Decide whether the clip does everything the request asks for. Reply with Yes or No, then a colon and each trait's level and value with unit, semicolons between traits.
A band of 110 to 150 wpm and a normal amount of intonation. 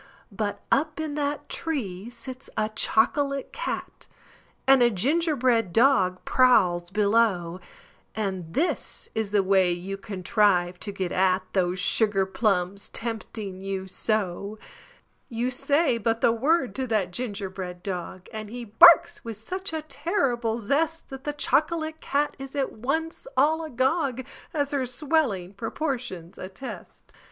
No: average, 140 wpm; wide, 6.3 semitones